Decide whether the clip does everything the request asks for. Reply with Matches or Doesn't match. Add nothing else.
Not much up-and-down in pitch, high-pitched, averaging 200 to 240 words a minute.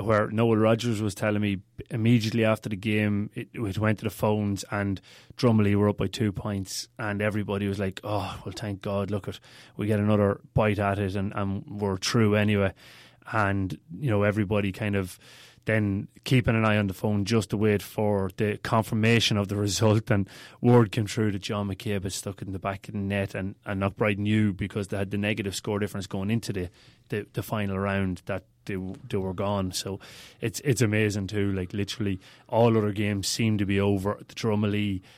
Doesn't match